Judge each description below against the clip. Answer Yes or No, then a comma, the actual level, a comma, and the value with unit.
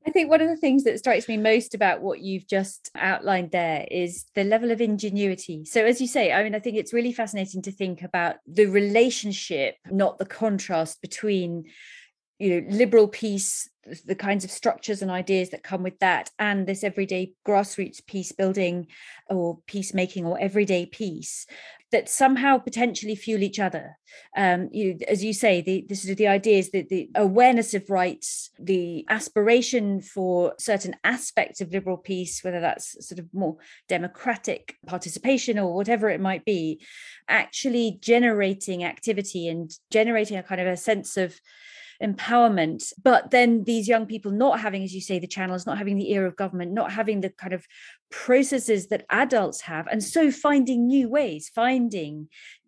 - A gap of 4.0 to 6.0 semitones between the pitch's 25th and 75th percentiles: No, average, 3.6 semitones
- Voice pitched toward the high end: Yes, high, 200 Hz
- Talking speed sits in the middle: Yes, average, 170 wpm